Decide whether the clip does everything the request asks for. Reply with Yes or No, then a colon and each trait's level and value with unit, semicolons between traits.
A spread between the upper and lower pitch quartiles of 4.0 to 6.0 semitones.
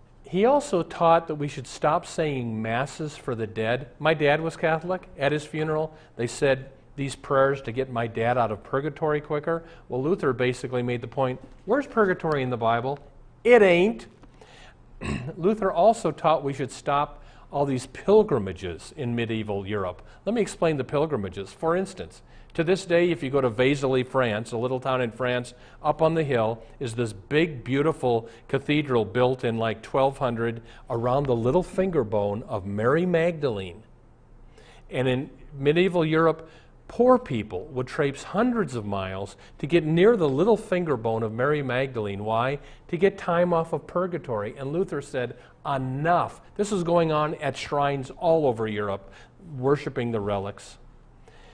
Yes: average, 5.2 semitones